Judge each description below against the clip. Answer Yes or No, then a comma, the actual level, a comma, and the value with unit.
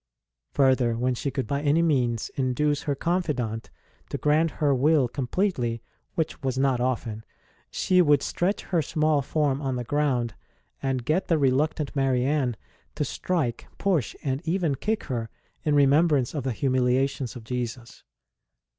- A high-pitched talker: No, low, 135 Hz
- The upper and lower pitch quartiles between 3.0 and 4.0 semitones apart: Yes, average, 3.4 semitones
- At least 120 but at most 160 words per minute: Yes, average, 155 wpm